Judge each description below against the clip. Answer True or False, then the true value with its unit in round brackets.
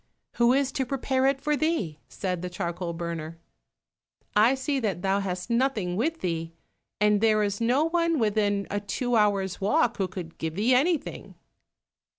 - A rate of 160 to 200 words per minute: True (165 wpm)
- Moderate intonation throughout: False (6.5 semitones)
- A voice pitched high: True (210 Hz)